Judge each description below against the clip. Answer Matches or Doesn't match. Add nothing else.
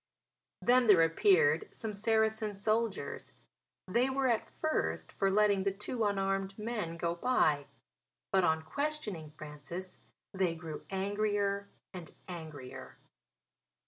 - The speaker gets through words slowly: Matches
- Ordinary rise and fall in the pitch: Matches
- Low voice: Doesn't match